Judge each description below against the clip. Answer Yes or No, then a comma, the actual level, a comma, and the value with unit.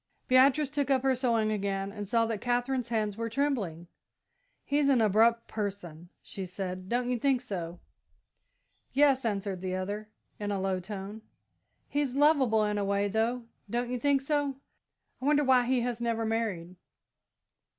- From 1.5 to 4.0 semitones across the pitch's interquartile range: No, average, 4.5 semitones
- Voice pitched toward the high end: Yes, high, 225 Hz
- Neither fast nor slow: Yes, average, 160 wpm